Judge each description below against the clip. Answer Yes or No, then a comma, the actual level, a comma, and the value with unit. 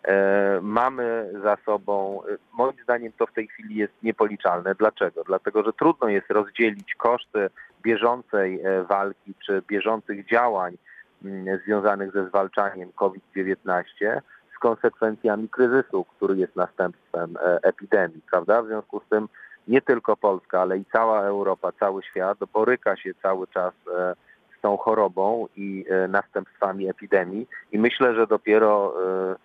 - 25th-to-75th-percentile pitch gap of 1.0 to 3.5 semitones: Yes, narrow, 2.6 semitones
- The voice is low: Yes, low, 100 Hz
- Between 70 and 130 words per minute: Yes, average, 125 wpm